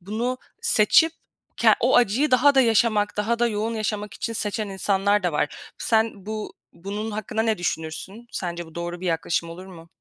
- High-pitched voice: Yes, high, 210 Hz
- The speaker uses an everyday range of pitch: Yes, average, 3.7 semitones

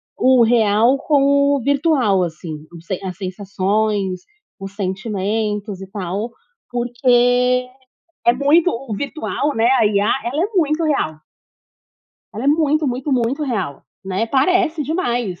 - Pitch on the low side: No, high, 235 Hz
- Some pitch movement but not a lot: No, wide, 5.9 semitones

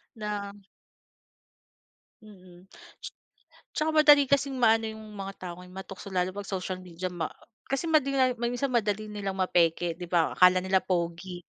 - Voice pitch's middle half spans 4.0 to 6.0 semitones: Yes, average, 4.5 semitones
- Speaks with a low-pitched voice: No, high, 195 Hz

